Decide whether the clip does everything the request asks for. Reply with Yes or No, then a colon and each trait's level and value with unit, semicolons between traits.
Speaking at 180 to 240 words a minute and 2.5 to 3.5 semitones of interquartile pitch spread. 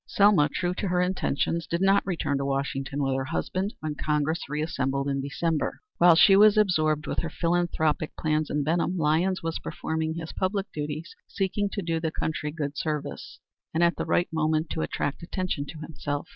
Yes: average, 185 wpm; average, 3.0 semitones